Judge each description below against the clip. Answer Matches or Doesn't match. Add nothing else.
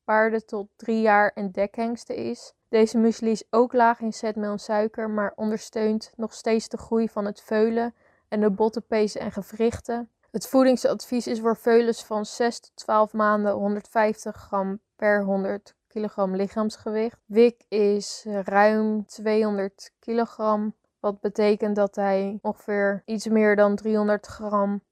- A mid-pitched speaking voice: Doesn't match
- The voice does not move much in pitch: Matches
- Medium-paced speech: Matches